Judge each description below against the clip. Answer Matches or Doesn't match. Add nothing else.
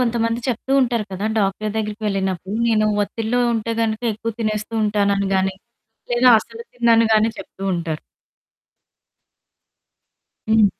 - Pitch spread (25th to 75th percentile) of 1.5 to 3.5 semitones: Matches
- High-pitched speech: Matches